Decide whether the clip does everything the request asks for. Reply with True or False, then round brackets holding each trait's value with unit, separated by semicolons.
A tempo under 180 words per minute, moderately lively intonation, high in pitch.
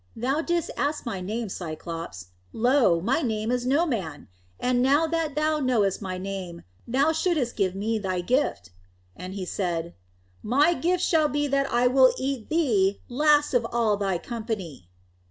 False (165 wpm; 7.1 semitones; 240 Hz)